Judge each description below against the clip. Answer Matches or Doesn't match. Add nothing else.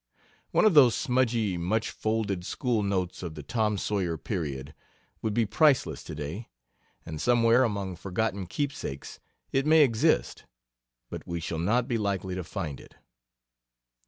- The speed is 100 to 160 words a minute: Matches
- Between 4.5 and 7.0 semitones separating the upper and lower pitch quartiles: Matches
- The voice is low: Matches